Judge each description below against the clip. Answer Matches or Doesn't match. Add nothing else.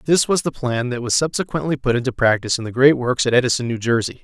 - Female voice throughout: Doesn't match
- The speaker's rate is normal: Doesn't match